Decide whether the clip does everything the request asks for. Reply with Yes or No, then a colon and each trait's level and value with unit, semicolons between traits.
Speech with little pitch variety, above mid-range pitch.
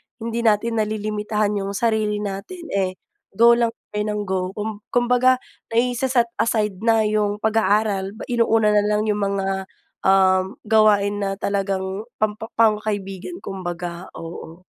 Yes: narrow, 2.3 semitones; high, 210 Hz